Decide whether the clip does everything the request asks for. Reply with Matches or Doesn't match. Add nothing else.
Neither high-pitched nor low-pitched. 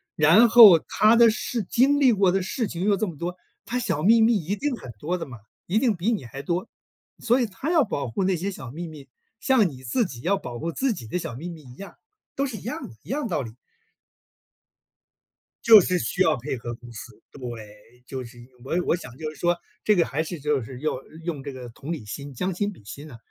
Matches